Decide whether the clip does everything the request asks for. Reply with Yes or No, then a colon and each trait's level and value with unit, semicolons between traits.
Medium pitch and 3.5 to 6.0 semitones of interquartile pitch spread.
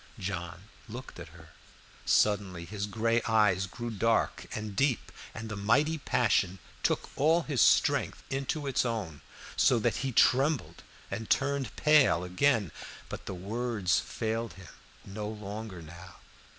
No: low, 110 Hz; average, 4.7 semitones